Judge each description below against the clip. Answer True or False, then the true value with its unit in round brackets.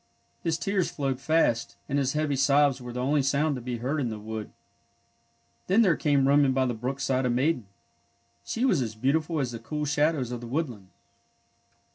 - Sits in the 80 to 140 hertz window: True (135 Hz)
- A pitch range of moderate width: True (3.5 semitones)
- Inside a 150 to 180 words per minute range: False (195 wpm)